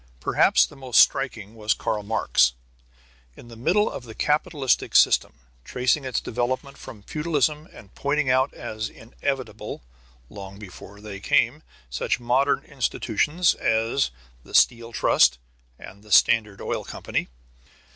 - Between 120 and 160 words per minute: Yes, slow, 135 wpm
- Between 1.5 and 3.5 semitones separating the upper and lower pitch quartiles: No, average, 4.5 semitones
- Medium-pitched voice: No, low, 120 Hz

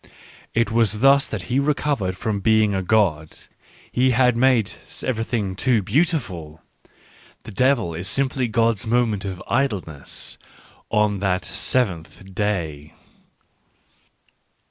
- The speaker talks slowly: Yes, slow, 115 wpm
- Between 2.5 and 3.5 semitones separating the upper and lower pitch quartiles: No, average, 4.9 semitones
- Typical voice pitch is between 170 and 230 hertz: No, low, 110 Hz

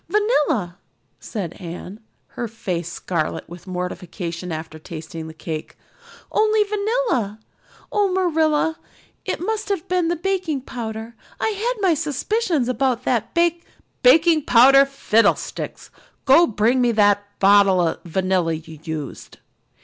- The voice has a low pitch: No, high, 240 Hz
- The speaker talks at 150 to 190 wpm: No, slow, 135 wpm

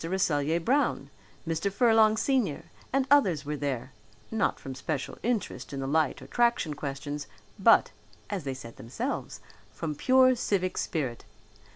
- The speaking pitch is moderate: Yes, medium, 160 Hz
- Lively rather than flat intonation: Yes, wide, 8.0 semitones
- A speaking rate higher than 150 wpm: No, average, 145 wpm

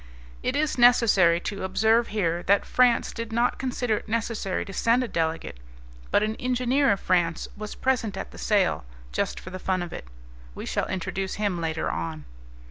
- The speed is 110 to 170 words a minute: No, average, 185 wpm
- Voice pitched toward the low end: No, high, 205 Hz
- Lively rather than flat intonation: No, average, 4.9 semitones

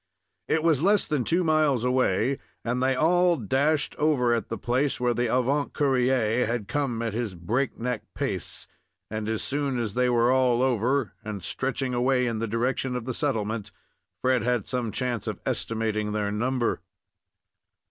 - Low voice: Yes, low, 125 Hz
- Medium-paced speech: Yes, average, 170 wpm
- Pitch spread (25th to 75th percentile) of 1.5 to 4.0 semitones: Yes, average, 2.9 semitones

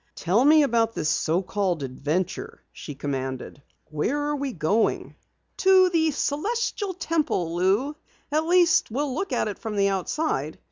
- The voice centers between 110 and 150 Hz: No, high, 230 Hz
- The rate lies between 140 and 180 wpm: Yes, average, 150 wpm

